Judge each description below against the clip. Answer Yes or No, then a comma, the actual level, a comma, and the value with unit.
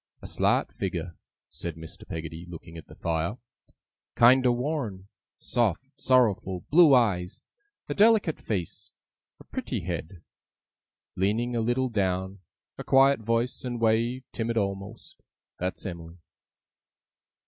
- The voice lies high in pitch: No, low, 105 Hz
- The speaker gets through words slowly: Yes, slow, 120 wpm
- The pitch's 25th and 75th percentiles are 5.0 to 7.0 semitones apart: Yes, wide, 5.5 semitones